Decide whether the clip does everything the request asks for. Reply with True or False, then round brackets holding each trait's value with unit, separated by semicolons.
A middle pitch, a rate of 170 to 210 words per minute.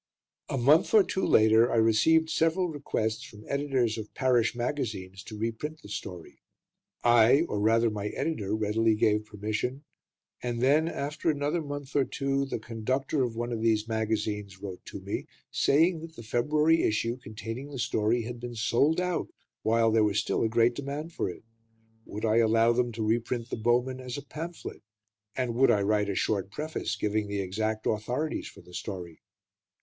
False (115 Hz; 180 wpm)